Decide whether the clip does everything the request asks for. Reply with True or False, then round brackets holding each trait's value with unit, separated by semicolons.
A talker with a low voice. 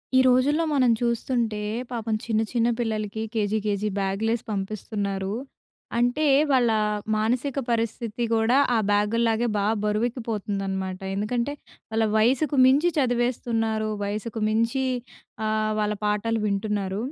False (225 Hz)